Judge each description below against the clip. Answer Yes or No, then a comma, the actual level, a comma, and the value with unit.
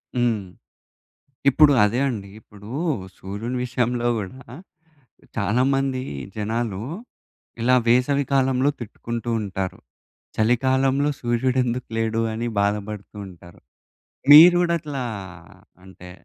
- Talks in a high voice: No, low, 120 Hz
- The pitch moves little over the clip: No, average, 3.8 semitones